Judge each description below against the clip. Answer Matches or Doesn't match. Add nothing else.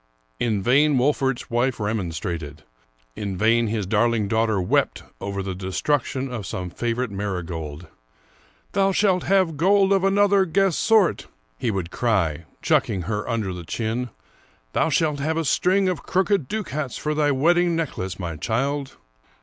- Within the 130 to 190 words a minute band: Matches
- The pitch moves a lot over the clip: Matches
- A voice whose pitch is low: Matches